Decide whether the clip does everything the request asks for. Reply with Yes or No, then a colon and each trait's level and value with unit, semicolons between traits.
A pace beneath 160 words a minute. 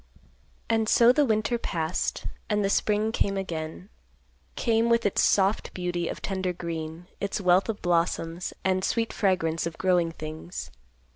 Yes: average, 150 wpm